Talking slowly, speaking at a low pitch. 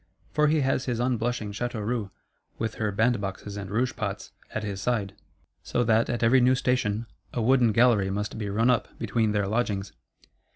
No: average, 180 wpm; low, 115 Hz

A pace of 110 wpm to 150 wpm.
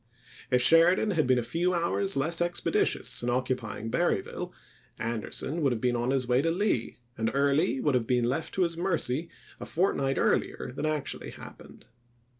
No: average, 175 wpm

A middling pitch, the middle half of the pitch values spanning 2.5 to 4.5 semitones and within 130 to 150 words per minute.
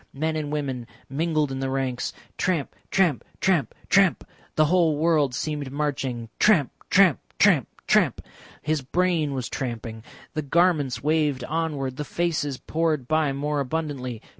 Yes: medium, 150 Hz; average, 3.2 semitones; average, 140 wpm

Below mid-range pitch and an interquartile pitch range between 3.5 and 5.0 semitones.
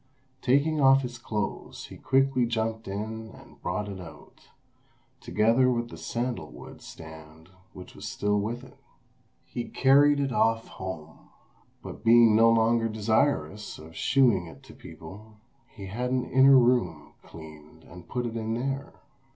Yes: low, 115 Hz; average, 4.1 semitones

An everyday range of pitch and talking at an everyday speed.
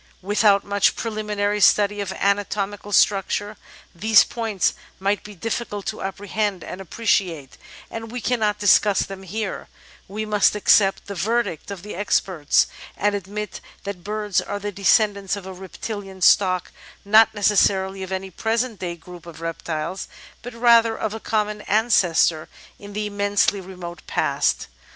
No: narrow, 1.8 semitones; average, 150 wpm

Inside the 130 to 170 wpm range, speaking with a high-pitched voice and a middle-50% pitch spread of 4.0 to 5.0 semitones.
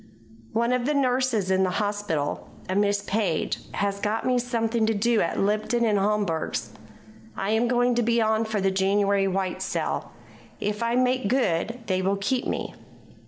No: average, 165 wpm; high, 210 Hz; average, 3.4 semitones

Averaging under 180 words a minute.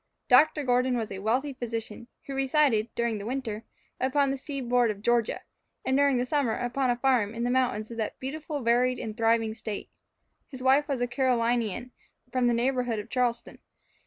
No: average, 185 wpm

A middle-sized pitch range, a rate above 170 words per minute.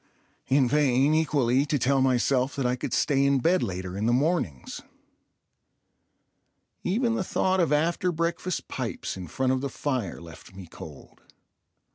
No: average, 4.7 semitones; average, 155 wpm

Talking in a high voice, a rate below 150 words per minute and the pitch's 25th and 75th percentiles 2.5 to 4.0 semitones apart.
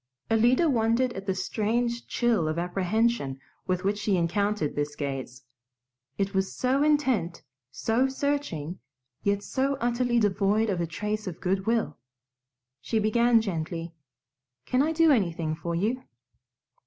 No: high, 210 Hz; average, 140 wpm; wide, 5.5 semitones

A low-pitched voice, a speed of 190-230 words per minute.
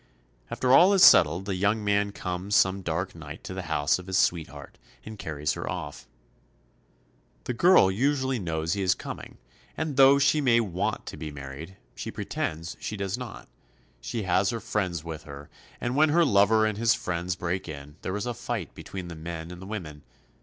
Yes: very low, 95 Hz; average, 195 wpm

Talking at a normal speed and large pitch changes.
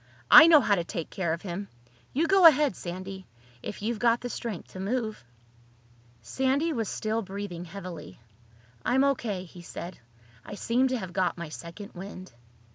Yes: average, 165 wpm; wide, 5.7 semitones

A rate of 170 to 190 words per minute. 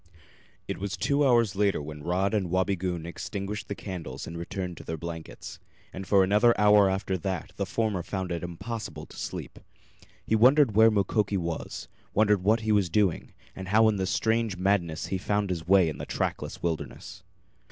Yes: average, 185 wpm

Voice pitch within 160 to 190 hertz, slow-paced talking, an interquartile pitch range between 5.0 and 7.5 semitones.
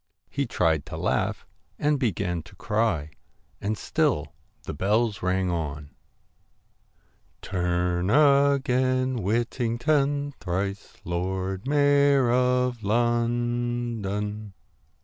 No: low, 115 Hz; slow, 90 wpm; wide, 5.6 semitones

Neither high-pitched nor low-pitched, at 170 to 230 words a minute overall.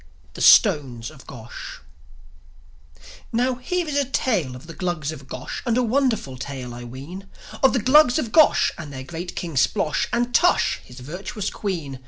Yes: medium, 175 Hz; average, 175 wpm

